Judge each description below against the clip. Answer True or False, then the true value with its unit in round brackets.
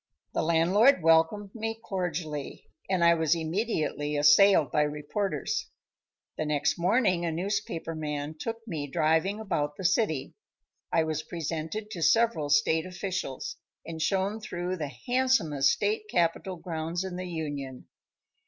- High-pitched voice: False (170 Hz)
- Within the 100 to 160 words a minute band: True (135 wpm)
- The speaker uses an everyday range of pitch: True (4.2 semitones)